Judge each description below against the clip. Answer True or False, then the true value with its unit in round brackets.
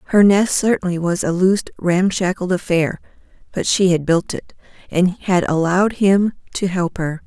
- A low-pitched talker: False (185 Hz)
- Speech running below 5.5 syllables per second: True (4.9 syllables/s)